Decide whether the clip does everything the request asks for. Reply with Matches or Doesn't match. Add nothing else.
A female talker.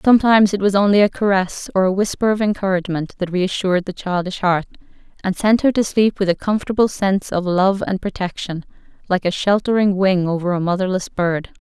Matches